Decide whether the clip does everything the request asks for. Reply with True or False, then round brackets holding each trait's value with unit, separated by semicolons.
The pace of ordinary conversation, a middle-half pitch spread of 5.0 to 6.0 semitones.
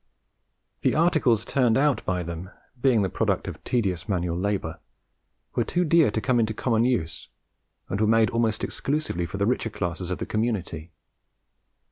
True (165 wpm; 5.4 semitones)